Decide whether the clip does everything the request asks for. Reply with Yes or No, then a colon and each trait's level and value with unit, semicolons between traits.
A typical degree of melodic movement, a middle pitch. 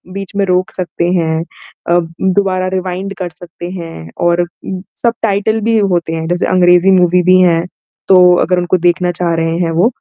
No: narrow, 1.4 semitones; medium, 180 Hz